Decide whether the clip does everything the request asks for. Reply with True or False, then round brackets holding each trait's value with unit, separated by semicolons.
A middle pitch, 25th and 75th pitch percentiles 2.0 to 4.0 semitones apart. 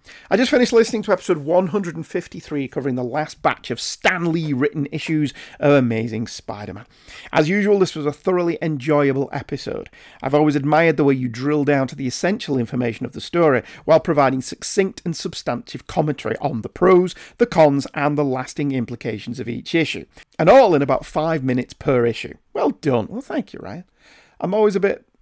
False (150 Hz; 4.7 semitones)